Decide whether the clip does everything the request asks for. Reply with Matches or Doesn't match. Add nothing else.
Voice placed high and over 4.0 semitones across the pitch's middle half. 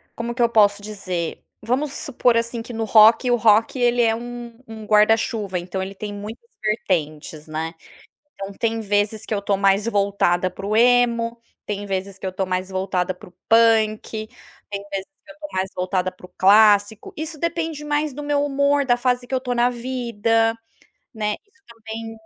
Doesn't match